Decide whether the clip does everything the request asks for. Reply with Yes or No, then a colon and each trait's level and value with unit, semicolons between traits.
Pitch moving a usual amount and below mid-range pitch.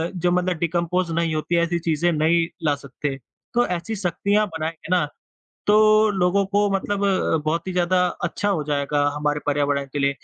No: average, 3.8 semitones; medium, 170 Hz